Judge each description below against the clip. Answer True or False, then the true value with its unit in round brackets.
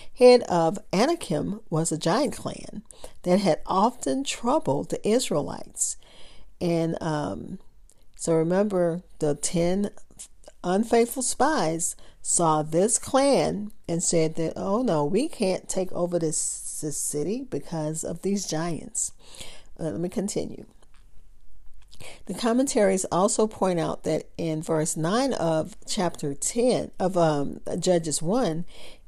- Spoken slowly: True (125 wpm)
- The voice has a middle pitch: True (180 Hz)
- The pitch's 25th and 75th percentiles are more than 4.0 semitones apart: True (4.6 semitones)